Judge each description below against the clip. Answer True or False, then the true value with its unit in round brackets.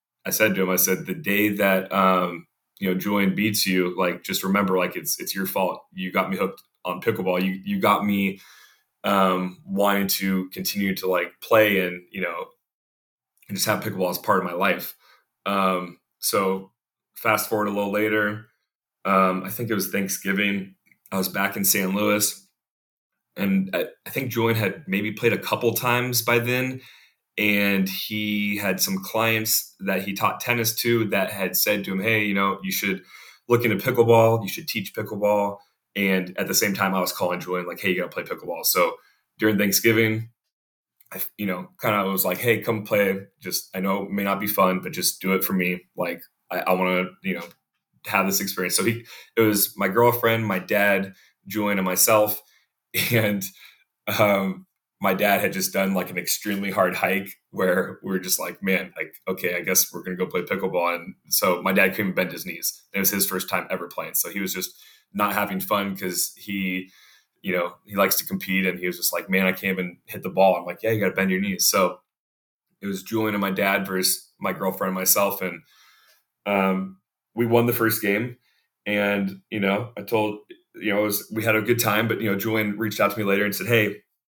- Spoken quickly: True (210 wpm)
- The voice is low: True (100 Hz)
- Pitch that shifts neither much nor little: False (2.3 semitones)